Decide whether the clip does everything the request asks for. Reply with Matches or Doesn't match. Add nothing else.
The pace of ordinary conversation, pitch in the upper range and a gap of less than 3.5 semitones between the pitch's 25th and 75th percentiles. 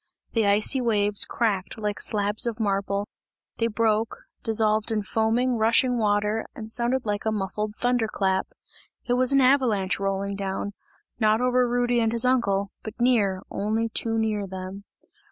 Matches